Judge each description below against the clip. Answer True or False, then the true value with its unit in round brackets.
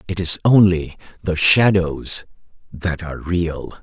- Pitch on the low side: True (85 Hz)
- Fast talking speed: False (125 wpm)